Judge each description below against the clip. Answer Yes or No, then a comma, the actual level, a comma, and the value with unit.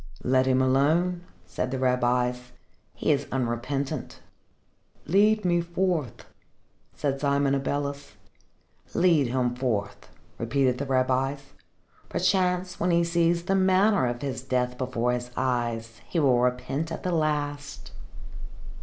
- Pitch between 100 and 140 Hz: Yes, low, 135 Hz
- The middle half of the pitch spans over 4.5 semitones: Yes, average, 5.2 semitones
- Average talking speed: No, slow, 125 wpm